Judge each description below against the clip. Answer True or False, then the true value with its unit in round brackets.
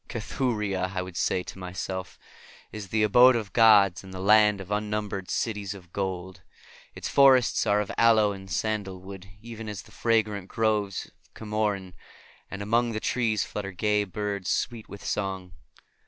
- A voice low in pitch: True (105 Hz)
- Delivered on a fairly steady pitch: True (2.3 semitones)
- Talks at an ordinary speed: True (160 wpm)